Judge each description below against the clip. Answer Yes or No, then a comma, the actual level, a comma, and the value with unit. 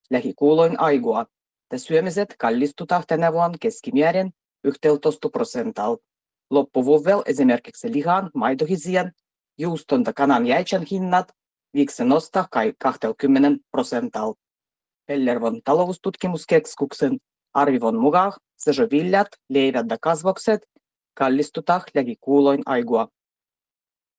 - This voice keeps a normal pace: No, slow, 90 wpm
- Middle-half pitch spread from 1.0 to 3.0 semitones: No, average, 4.8 semitones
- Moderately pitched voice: Yes, medium, 160 Hz